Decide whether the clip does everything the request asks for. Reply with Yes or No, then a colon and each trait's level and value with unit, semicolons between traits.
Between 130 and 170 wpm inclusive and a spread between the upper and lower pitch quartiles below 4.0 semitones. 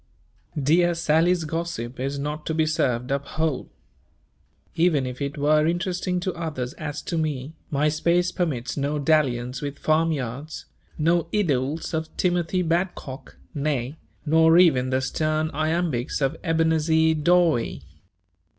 Yes: slow, 135 wpm; average, 3.0 semitones